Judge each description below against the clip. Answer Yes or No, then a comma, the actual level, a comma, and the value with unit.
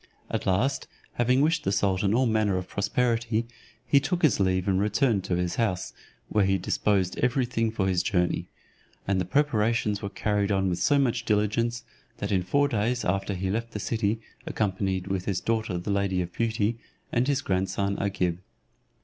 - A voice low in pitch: Yes, low, 105 Hz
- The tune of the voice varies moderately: Yes, average, 3.5 semitones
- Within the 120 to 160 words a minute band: No, average, 185 wpm